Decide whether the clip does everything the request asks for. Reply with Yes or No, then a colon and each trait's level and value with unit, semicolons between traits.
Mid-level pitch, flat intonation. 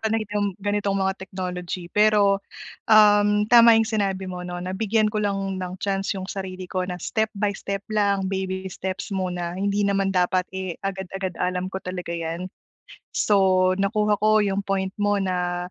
No: high, 195 Hz; narrow, 1.8 semitones